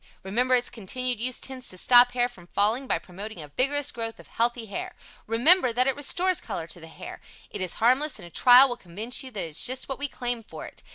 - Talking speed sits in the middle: No, fast, 240 wpm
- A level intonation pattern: No, average, 3.8 semitones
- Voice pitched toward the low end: No, high, 245 Hz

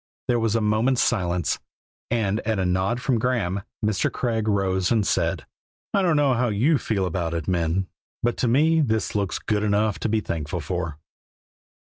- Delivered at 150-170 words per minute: No, average, 180 wpm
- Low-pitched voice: Yes, low, 105 Hz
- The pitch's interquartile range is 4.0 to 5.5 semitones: Yes, average, 4.4 semitones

